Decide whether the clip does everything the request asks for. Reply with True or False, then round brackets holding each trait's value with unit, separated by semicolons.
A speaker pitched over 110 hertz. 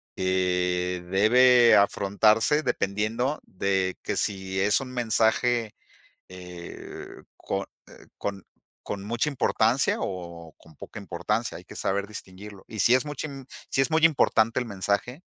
False (105 Hz)